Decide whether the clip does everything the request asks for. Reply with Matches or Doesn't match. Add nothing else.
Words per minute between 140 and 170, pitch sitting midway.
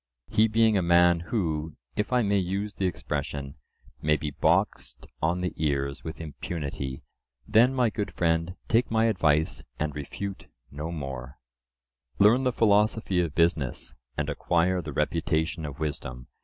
Doesn't match